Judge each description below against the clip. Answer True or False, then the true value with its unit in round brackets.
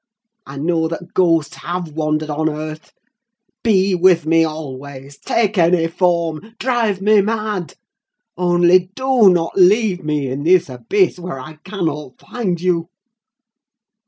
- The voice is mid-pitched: True (175 Hz)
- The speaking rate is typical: False (125 wpm)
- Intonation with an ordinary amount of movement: True (3.5 semitones)